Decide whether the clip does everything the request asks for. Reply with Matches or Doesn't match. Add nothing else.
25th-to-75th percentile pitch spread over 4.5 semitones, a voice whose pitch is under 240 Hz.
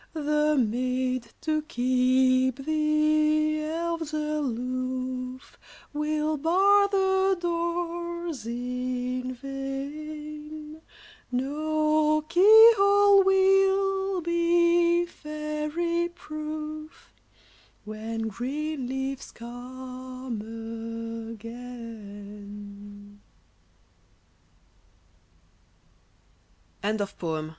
Doesn't match